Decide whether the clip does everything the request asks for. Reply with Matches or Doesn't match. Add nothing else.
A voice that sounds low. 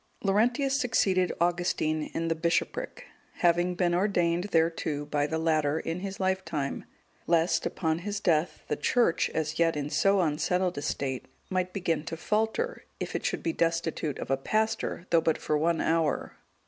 Doesn't match